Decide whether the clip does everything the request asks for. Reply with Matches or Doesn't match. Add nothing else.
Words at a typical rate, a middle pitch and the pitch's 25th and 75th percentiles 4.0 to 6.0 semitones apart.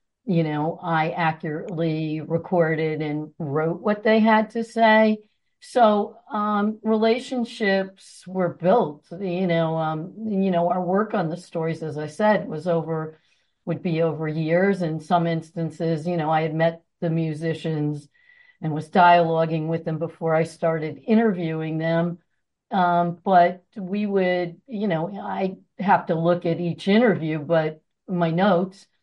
Doesn't match